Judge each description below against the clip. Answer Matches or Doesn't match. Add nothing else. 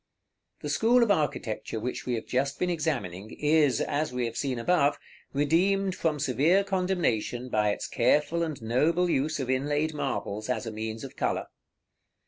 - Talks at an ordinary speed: Matches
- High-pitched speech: Doesn't match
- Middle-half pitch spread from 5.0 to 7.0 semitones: Matches